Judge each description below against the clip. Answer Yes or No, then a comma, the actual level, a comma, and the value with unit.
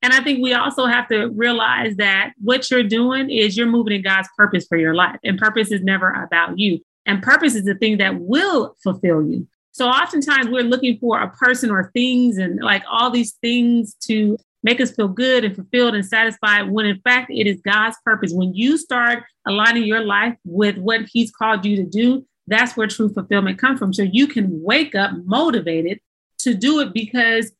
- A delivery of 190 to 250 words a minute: Yes, fast, 205 wpm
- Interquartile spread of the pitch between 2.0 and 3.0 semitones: No, average, 3.5 semitones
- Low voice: No, high, 225 Hz